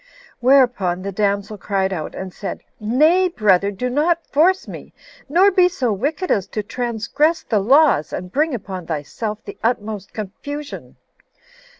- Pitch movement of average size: No, wide, 7.1 semitones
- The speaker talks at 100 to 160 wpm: Yes, average, 150 wpm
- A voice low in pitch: No, high, 225 Hz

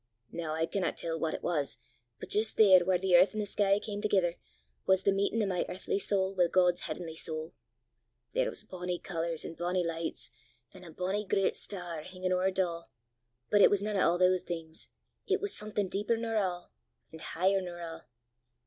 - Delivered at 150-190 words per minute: No, fast, 205 wpm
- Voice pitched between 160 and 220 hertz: Yes, medium, 185 Hz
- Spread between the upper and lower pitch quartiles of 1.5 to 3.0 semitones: Yes, average, 2.7 semitones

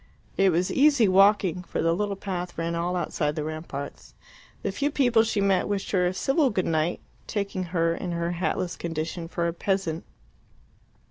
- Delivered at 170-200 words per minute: Yes, average, 180 wpm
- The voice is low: No, medium, 180 Hz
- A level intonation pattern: No, average, 3.0 semitones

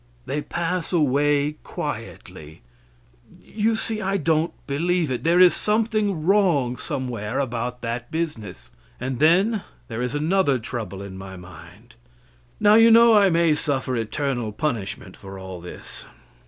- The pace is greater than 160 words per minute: No, average, 140 wpm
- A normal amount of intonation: No, wide, 7.5 semitones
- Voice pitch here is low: No, medium, 145 Hz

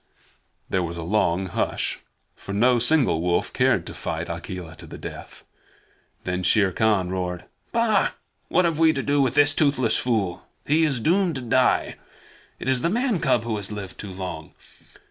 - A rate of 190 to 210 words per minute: No, average, 180 wpm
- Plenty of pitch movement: Yes, wide, 7.8 semitones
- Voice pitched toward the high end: No, low, 115 Hz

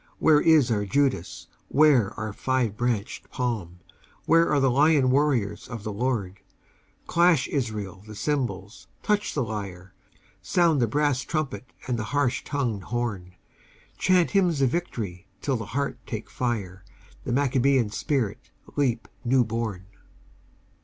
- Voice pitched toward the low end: Yes, low, 125 Hz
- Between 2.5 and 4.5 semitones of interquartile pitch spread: No, average, 5.3 semitones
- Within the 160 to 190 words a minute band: No, average, 140 wpm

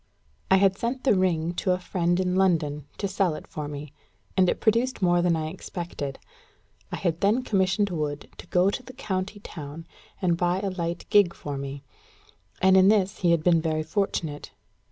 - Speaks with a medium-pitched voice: Yes, medium, 180 Hz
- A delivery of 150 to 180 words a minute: No, average, 195 wpm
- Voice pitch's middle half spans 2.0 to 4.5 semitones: Yes, average, 3.3 semitones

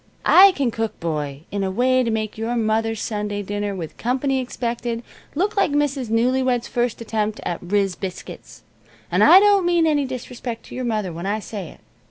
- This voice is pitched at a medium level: No, high, 230 Hz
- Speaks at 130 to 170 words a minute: No, average, 190 wpm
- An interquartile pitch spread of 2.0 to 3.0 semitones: No, average, 4.0 semitones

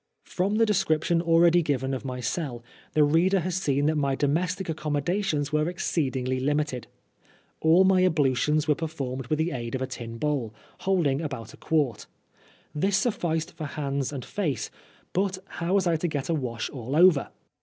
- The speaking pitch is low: No, medium, 150 Hz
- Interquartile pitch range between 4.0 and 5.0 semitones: Yes, average, 4.4 semitones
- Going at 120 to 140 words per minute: No, average, 175 wpm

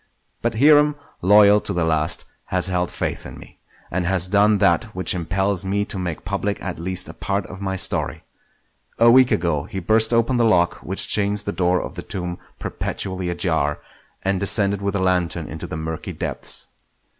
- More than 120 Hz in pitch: No, very low, 95 Hz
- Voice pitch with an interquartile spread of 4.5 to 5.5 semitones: No, average, 2.7 semitones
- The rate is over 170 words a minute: Yes, average, 190 wpm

